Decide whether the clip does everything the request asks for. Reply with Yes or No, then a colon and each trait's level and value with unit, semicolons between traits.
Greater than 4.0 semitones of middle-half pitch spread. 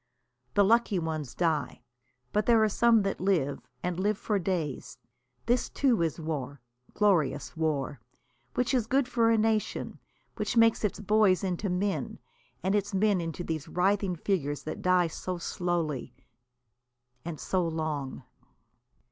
Yes: average, 4.8 semitones